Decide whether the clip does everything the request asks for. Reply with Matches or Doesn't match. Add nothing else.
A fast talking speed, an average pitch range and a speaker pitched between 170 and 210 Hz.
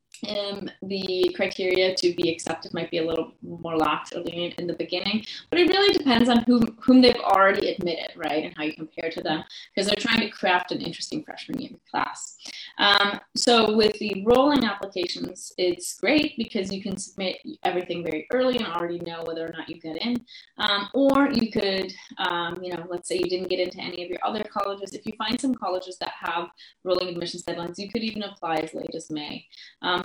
Matches